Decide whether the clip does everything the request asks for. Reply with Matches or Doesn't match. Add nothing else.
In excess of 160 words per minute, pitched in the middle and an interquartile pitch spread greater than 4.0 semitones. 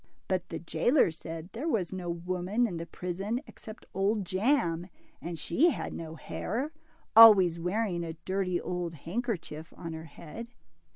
Doesn't match